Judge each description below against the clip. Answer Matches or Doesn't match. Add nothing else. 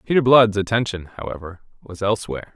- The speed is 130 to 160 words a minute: Matches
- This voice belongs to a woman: Doesn't match